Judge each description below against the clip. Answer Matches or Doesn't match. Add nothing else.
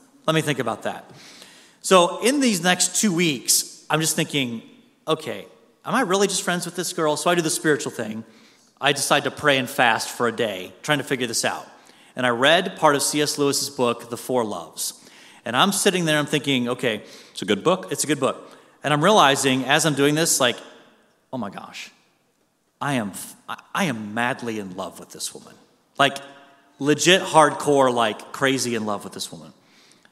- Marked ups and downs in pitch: Doesn't match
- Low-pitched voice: Doesn't match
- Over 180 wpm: Matches